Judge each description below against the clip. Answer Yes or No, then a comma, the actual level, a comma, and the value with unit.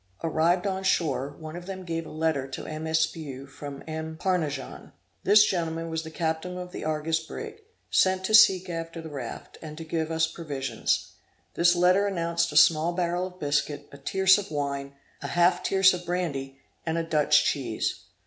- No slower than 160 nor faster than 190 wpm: Yes, average, 185 wpm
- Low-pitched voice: No, medium, 165 Hz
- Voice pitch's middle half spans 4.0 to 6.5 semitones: No, average, 2.9 semitones